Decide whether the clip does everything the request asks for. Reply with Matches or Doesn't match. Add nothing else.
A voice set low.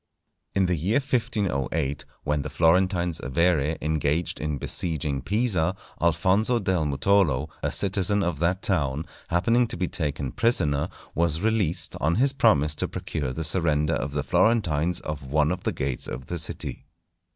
Matches